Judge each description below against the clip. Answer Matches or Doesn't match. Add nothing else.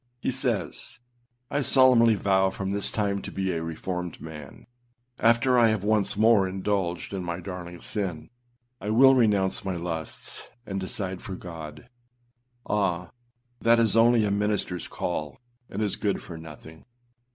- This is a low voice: Matches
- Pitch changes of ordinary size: Matches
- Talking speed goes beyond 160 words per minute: Doesn't match